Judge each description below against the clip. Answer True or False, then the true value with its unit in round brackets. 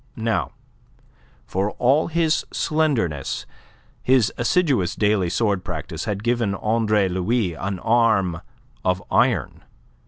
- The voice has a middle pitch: False (110 Hz)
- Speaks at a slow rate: True (105 wpm)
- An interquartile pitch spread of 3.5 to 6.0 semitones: True (4.3 semitones)